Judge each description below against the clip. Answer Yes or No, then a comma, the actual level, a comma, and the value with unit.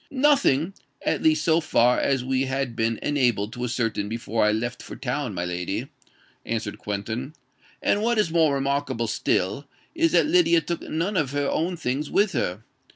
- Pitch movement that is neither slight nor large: No, wide, 6.4 semitones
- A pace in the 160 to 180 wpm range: Yes, average, 170 wpm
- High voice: No, low, 135 Hz